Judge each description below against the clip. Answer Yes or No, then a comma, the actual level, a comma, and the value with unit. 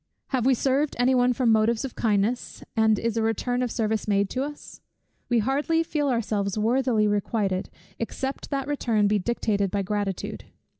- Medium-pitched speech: No, high, 230 Hz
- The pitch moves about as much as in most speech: Yes, average, 3.7 semitones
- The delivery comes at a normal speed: Yes, average, 170 wpm